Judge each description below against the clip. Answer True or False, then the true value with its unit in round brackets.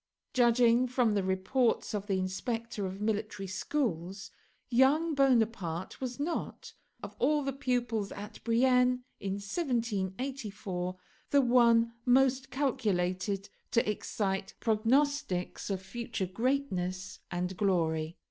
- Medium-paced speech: False (110 wpm)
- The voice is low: False (225 Hz)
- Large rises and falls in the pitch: False (4.9 semitones)